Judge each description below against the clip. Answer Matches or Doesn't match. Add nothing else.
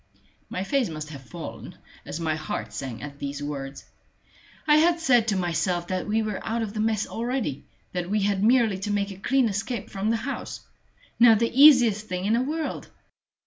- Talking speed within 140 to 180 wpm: Doesn't match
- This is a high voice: Matches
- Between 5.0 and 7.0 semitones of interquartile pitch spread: Matches